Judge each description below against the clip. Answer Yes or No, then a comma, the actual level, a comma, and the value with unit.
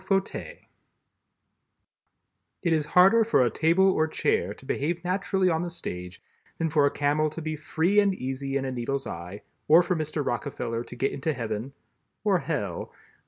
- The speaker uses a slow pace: No, average, 170 wpm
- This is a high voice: No, medium, 155 Hz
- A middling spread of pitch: Yes, average, 4.9 semitones